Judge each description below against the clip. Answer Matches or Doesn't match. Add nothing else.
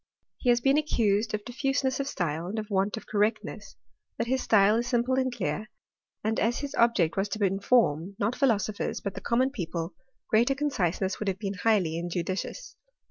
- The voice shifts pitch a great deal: Doesn't match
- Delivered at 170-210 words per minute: Matches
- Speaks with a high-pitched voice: Matches